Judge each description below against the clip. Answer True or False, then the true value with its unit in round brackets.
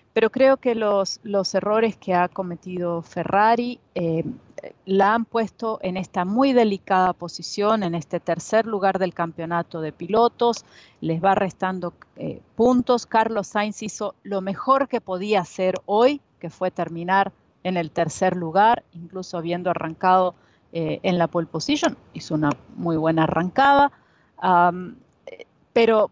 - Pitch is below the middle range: False (190 Hz)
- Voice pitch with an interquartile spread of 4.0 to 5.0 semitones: True (4.4 semitones)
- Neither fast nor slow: True (145 wpm)